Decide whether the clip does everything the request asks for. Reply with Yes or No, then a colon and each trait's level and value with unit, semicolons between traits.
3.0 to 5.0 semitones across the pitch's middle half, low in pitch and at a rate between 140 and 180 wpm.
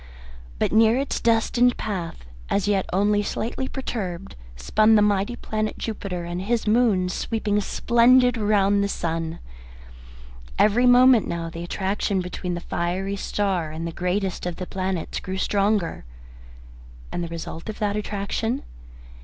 No: average, 3.5 semitones; high, 200 Hz; average, 145 wpm